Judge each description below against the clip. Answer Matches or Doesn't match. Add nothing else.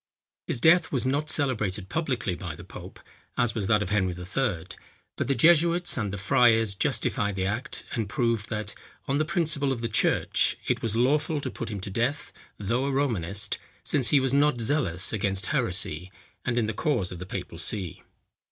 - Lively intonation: Matches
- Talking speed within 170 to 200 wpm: Matches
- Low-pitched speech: Matches